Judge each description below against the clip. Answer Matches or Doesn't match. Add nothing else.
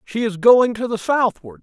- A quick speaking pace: Matches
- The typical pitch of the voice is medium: Doesn't match